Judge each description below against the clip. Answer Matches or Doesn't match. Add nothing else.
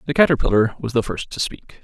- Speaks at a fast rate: Matches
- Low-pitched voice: Matches